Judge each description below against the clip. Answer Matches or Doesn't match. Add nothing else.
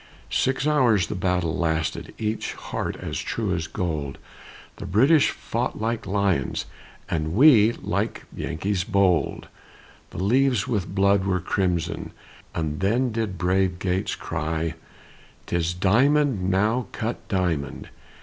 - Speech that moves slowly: Matches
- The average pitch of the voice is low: Matches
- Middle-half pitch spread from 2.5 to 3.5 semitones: Doesn't match